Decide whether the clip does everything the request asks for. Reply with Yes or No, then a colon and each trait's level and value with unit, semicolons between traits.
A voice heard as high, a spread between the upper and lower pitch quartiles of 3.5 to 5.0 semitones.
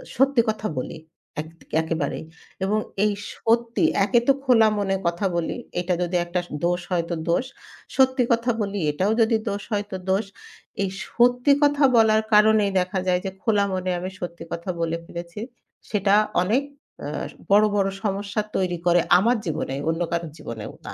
Yes: high, 200 Hz; average, 4.2 semitones